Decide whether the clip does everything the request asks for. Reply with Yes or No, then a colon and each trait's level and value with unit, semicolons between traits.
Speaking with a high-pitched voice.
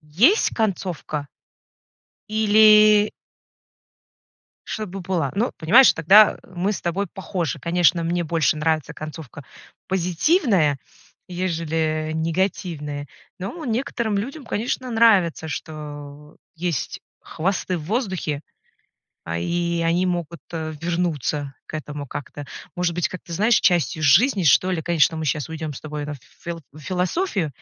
No: medium, 170 Hz